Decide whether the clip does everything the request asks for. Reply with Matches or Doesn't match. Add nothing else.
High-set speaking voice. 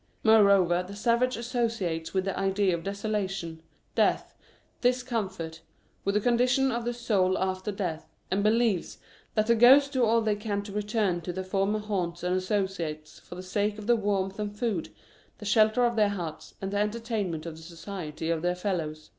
Matches